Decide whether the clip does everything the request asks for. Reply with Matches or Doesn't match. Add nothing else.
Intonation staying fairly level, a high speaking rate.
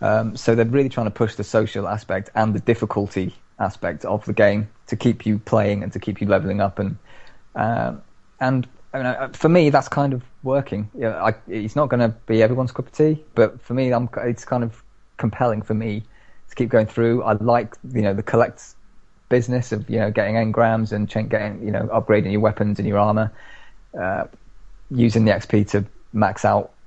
Matches